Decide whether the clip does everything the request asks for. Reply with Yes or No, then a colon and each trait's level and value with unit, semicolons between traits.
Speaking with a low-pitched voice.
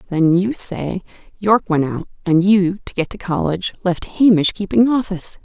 No: high, 190 Hz